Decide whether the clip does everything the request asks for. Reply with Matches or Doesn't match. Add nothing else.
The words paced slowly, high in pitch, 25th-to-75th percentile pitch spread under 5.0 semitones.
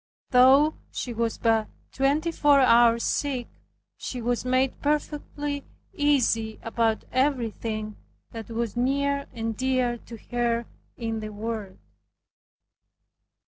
Matches